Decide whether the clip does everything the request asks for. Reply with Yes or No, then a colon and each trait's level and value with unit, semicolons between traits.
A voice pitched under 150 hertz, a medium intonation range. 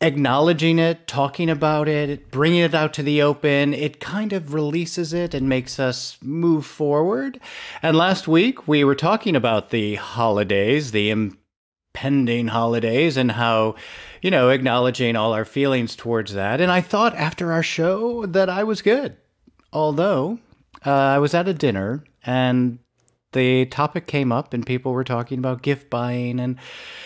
Yes: medium, 140 Hz; average, 5.0 semitones